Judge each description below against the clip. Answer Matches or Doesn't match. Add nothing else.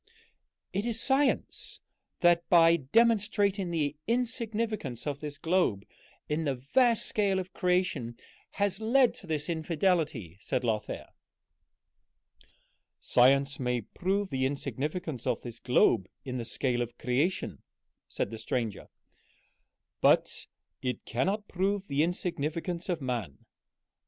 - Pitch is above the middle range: Doesn't match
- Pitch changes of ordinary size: Doesn't match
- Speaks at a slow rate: Matches